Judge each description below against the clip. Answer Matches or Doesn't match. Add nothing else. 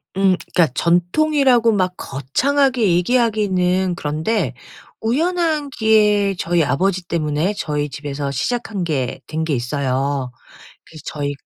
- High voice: Doesn't match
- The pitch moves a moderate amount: Doesn't match